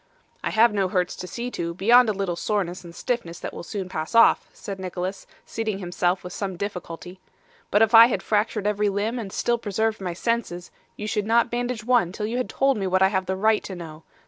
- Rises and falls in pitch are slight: No, average, 3.7 semitones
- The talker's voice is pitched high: Yes, high, 200 Hz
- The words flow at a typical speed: No, fast, 225 wpm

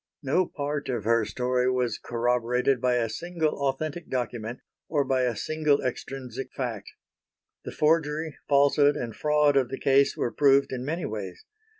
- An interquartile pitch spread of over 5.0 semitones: No, average, 3.2 semitones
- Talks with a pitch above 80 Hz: Yes, low, 135 Hz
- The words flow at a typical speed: Yes, average, 160 wpm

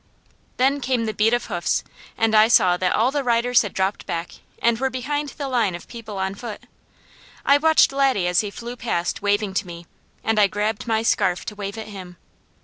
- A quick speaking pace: Yes, fast, 210 wpm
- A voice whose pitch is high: Yes, high, 220 Hz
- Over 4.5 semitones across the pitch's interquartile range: No, average, 3.9 semitones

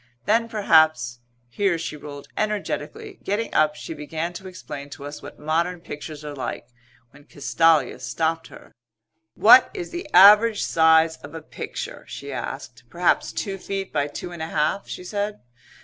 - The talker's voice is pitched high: No, medium, 165 Hz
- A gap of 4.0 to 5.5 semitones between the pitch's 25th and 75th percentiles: Yes, average, 5.1 semitones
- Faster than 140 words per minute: Yes, average, 165 wpm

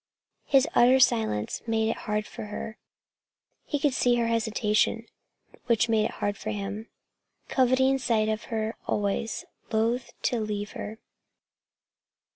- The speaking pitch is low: No, high, 220 Hz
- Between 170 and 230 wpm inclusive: No, slow, 135 wpm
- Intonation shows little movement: Yes, narrow, 2.3 semitones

